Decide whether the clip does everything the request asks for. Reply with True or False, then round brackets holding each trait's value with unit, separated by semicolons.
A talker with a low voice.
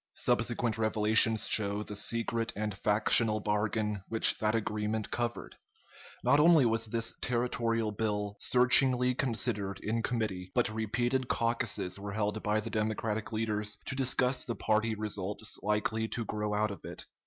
True (110 Hz)